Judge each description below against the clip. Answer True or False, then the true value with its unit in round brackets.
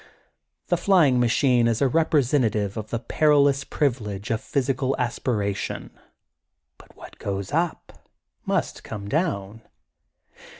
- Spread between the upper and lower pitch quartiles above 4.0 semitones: True (4.9 semitones)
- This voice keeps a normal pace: False (125 wpm)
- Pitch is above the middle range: False (125 Hz)